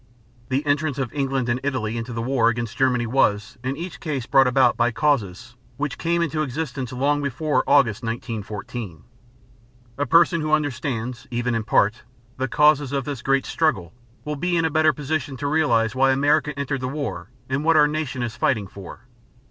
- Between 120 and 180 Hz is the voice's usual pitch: Yes, low, 135 Hz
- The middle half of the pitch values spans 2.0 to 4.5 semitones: Yes, average, 3.8 semitones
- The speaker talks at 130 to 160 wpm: No, average, 185 wpm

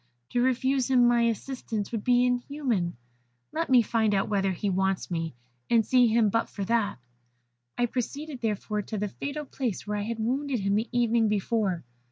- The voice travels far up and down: No, average, 3.3 semitones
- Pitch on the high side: Yes, high, 230 Hz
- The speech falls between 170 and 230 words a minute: Yes, average, 185 wpm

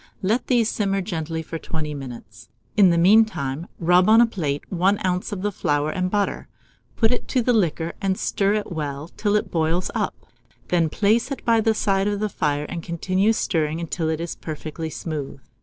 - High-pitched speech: No, medium, 180 Hz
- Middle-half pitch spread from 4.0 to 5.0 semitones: Yes, average, 4.6 semitones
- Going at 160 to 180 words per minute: No, average, 195 wpm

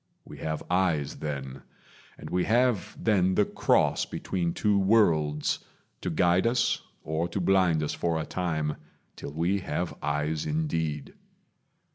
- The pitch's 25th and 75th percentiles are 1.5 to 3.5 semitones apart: No, average, 3.9 semitones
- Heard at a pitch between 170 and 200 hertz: No, very low, 85 Hz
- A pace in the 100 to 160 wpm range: Yes, average, 140 wpm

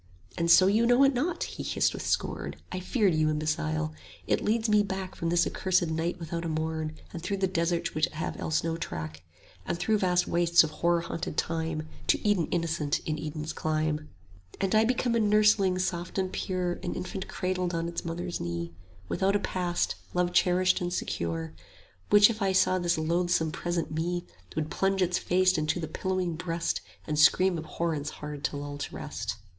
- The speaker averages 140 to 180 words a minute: No, average, 195 wpm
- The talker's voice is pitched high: No, medium, 175 Hz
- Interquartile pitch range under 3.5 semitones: Yes, average, 2.9 semitones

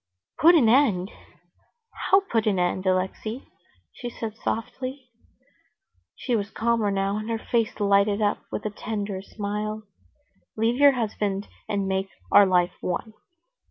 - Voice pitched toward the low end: No, high, 215 Hz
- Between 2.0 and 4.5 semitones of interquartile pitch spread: Yes, average, 2.7 semitones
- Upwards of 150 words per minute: No, average, 140 wpm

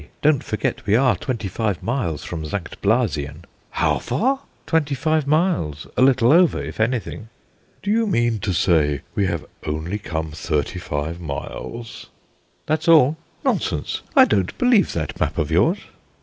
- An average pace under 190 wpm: Yes, average, 155 wpm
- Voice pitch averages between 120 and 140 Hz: No, low, 110 Hz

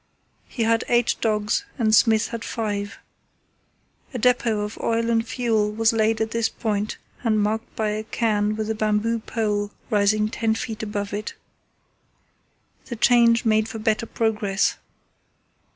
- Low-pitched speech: No, high, 220 Hz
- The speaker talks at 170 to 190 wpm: No, average, 150 wpm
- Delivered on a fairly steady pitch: Yes, narrow, 1.4 semitones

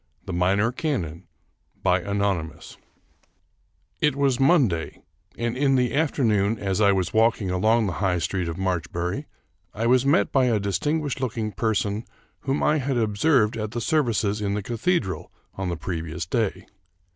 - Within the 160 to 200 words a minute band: No, average, 150 wpm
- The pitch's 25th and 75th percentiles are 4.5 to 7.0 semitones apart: Yes, average, 5.3 semitones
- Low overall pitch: Yes, low, 110 Hz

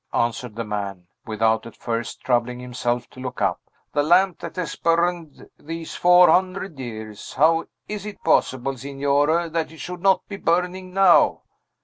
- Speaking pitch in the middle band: Yes, medium, 150 Hz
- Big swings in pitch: Yes, wide, 6.7 semitones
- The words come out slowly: No, average, 160 wpm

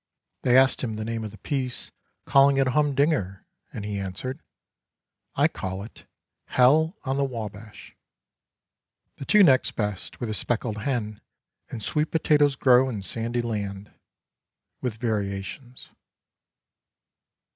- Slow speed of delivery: No, average, 145 wpm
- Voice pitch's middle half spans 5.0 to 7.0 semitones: No, average, 4.4 semitones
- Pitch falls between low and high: No, low, 120 Hz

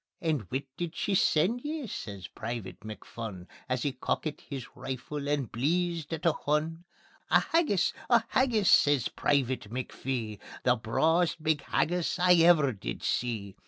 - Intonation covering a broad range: Yes, wide, 6.3 semitones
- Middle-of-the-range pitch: Yes, medium, 145 Hz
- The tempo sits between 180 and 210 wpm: No, average, 150 wpm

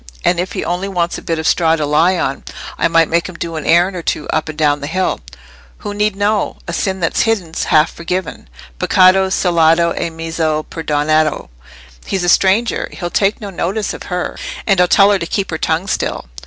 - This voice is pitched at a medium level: Yes, medium, 170 Hz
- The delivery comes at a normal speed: No, fast, 210 wpm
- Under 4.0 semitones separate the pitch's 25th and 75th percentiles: Yes, average, 2.8 semitones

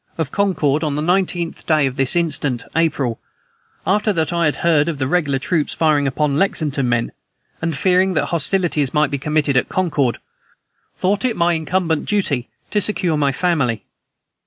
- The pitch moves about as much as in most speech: Yes, average, 4.0 semitones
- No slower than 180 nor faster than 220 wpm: No, average, 170 wpm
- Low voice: No, medium, 155 Hz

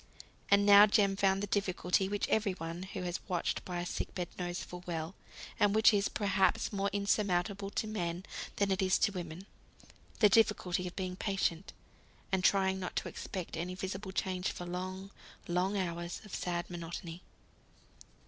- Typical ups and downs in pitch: No, narrow, 2.1 semitones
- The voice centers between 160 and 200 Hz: Yes, high, 190 Hz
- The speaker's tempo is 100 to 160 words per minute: No, average, 170 wpm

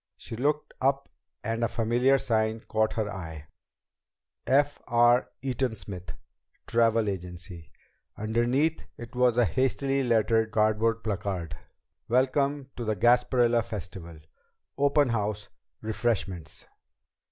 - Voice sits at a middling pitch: No, low, 115 Hz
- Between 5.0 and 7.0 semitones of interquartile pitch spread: No, average, 3.4 semitones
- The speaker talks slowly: Yes, slow, 110 wpm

